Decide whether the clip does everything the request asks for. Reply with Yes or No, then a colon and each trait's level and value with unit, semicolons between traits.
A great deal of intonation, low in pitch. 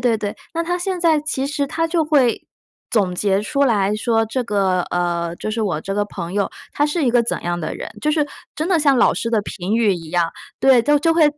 No: wide, 7.1 semitones; high, 230 Hz